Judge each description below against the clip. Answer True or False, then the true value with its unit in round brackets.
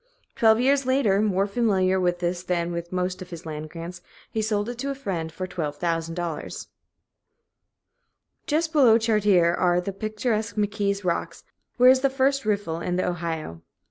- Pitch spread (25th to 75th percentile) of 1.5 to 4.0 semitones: False (4.4 semitones)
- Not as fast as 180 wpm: True (165 wpm)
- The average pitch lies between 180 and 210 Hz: True (190 Hz)